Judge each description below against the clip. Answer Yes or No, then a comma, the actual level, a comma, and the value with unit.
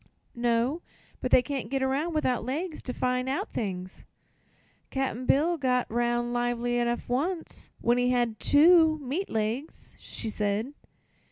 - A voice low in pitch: No, very high, 250 Hz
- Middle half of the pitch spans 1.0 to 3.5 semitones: Yes, average, 3.2 semitones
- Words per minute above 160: No, average, 145 wpm